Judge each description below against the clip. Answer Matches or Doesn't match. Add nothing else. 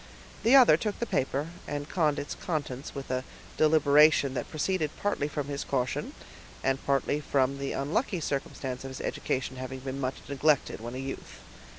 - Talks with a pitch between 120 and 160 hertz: Matches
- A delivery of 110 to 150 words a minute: Doesn't match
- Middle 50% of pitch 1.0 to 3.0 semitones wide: Matches